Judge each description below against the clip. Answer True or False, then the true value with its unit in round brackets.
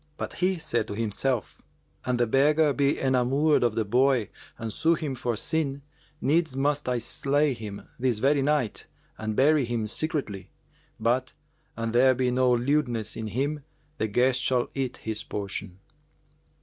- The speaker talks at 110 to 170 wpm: True (160 wpm)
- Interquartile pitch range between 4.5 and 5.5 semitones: False (3.9 semitones)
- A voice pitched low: True (130 Hz)